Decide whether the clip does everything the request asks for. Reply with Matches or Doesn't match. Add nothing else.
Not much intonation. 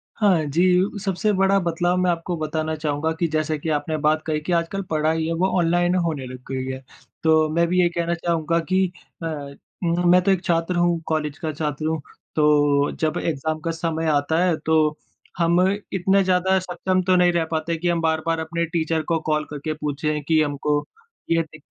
Matches